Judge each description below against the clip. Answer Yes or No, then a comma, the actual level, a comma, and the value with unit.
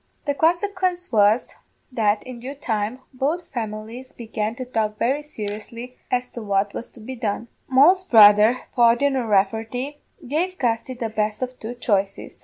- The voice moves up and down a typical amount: Yes, average, 3.7 semitones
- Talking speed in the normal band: Yes, average, 155 wpm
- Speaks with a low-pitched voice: No, high, 235 Hz